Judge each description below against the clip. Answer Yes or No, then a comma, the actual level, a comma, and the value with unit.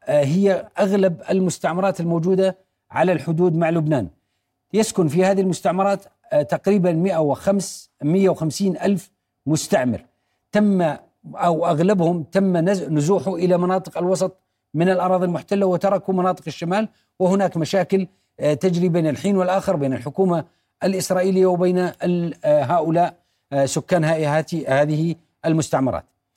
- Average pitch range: Yes, average, 3.1 semitones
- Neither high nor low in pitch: Yes, medium, 180 Hz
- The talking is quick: No, average, 105 wpm